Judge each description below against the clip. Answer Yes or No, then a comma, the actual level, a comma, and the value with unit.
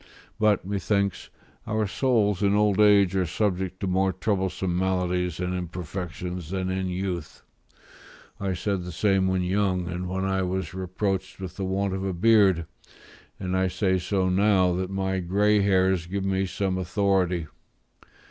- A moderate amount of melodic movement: No, narrow, 1.5 semitones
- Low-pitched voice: Yes, very low, 95 Hz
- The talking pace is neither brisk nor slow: Yes, average, 155 wpm